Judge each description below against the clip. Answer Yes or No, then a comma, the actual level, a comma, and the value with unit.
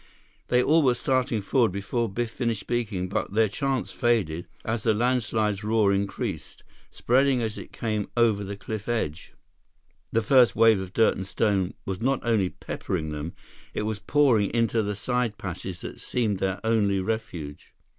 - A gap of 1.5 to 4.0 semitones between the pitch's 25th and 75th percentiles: Yes, average, 3.3 semitones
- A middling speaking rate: Yes, average, 165 wpm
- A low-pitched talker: Yes, low, 110 Hz